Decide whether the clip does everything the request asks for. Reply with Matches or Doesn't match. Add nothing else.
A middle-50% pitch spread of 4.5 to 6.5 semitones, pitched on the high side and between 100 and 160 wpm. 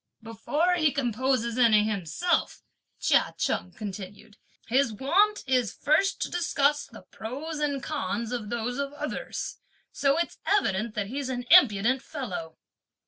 Matches